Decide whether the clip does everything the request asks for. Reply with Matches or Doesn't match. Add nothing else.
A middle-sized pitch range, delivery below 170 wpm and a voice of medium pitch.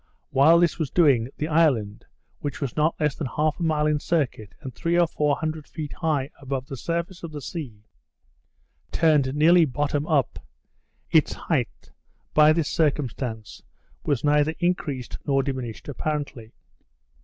Matches